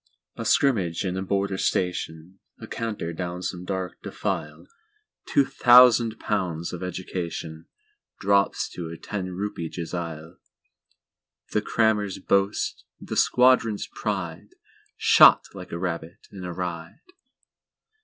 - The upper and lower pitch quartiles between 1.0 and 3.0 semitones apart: No, average, 3.6 semitones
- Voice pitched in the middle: No, very low, 95 Hz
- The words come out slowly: Yes, slow, 105 wpm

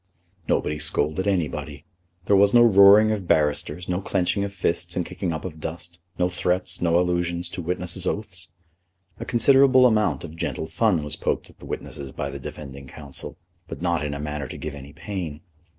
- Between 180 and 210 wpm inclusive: Yes, average, 185 wpm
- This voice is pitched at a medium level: No, very low, 85 Hz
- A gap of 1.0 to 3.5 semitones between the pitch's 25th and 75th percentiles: No, average, 4.3 semitones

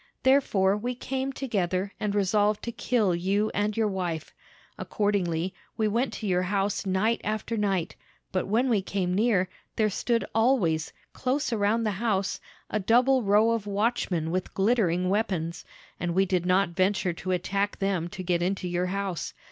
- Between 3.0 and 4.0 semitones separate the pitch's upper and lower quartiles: Yes, average, 3.3 semitones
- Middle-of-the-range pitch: No, high, 200 Hz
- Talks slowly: No, average, 165 wpm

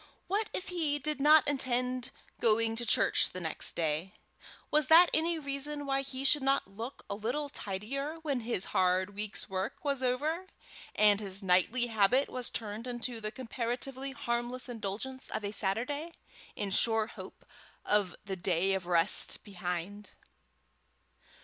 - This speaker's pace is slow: No, average, 150 wpm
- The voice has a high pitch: Yes, high, 240 Hz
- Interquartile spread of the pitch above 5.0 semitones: Yes, wide, 5.5 semitones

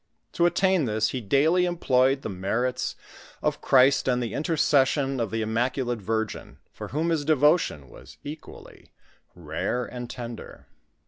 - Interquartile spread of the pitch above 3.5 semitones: Yes, average, 4.8 semitones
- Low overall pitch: Yes, low, 130 Hz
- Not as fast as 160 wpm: Yes, average, 140 wpm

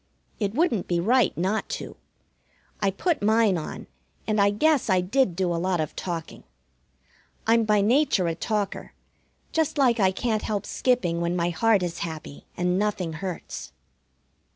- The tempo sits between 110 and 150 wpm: No, average, 160 wpm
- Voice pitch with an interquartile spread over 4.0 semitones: Yes, average, 4.5 semitones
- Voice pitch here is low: No, high, 200 Hz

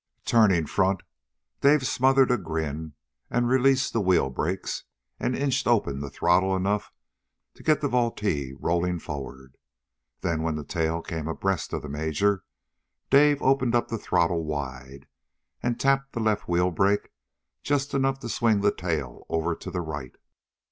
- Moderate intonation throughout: No, wide, 7.4 semitones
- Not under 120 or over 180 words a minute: Yes, average, 155 wpm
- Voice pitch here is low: Yes, very low, 95 Hz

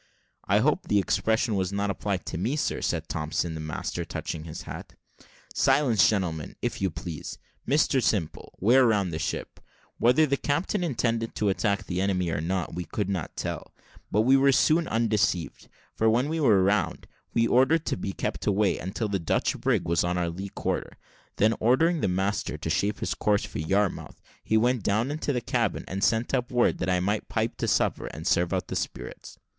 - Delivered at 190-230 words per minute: Yes, average, 200 wpm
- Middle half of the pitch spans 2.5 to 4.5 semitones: No, average, 5.0 semitones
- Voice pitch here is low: Yes, low, 105 Hz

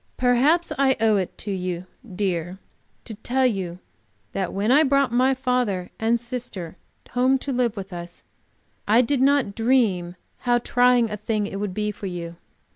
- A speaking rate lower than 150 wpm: No, average, 170 wpm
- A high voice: Yes, high, 225 Hz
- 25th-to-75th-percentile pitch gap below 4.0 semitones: No, average, 4.7 semitones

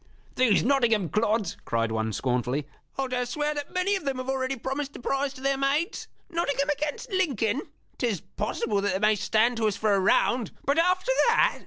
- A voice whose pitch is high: Yes, very high, 255 Hz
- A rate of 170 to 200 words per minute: Yes, average, 195 wpm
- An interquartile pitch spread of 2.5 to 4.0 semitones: No, average, 5.2 semitones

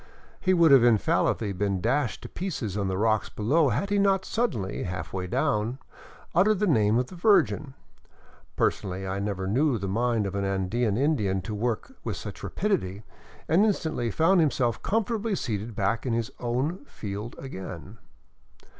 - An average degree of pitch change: No, wide, 8.3 semitones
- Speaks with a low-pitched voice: Yes, low, 115 Hz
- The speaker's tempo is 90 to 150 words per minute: No, average, 170 wpm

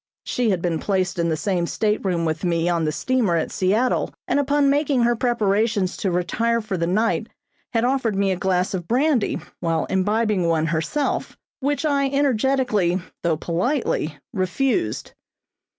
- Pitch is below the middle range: No, high, 200 Hz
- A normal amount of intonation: No, wide, 6.2 semitones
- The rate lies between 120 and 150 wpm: No, average, 160 wpm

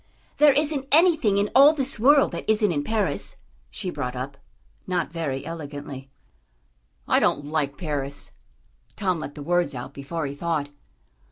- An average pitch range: No, wide, 7.6 semitones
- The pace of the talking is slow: No, average, 155 wpm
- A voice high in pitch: No, medium, 165 Hz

